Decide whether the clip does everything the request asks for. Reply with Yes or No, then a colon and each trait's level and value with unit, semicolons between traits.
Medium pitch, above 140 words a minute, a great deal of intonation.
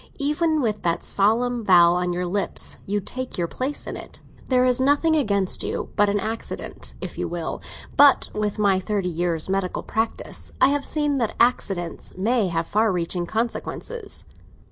No: high, 210 Hz; average, 170 wpm; wide, 5.9 semitones